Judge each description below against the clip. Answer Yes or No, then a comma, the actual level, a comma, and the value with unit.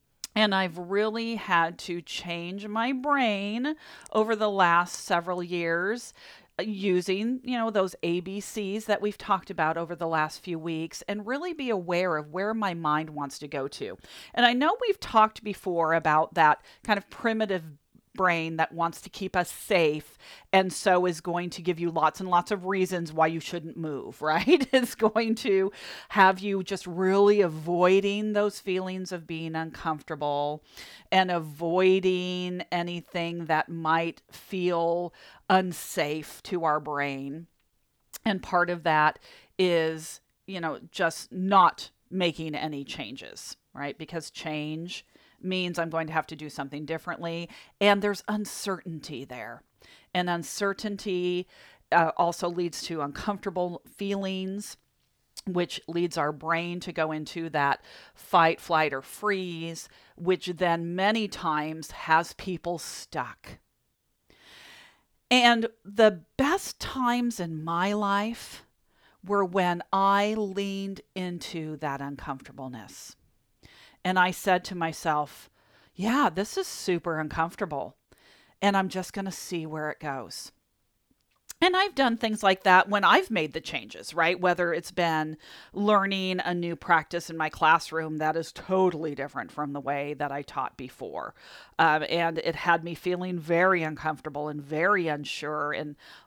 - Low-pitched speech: No, medium, 175 Hz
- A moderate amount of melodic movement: Yes, average, 3.7 semitones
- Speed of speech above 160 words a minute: No, average, 145 wpm